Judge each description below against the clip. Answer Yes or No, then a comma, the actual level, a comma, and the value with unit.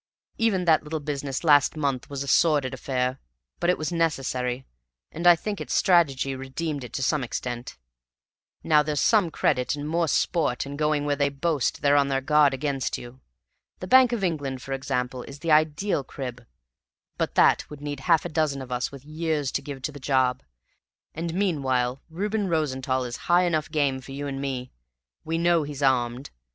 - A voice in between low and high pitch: Yes, medium, 145 Hz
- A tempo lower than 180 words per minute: No, average, 190 wpm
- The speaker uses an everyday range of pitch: Yes, average, 3.4 semitones